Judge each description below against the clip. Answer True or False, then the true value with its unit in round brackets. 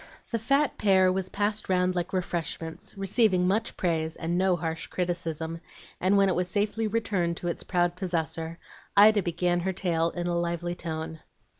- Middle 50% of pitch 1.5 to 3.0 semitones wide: True (2.5 semitones)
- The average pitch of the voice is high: False (180 Hz)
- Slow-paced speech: False (170 wpm)